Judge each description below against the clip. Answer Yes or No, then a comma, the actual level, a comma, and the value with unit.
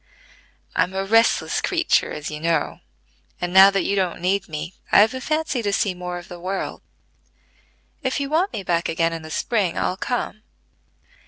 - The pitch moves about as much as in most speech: Yes, average, 4.2 semitones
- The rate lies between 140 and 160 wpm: No, average, 180 wpm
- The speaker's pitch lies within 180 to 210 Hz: Yes, high, 190 Hz